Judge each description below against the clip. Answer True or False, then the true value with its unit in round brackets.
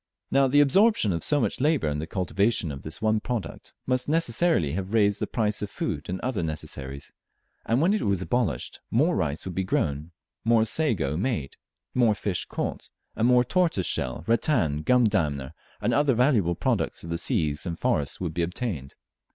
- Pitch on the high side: False (100 Hz)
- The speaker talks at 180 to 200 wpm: True (190 wpm)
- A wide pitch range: True (7.9 semitones)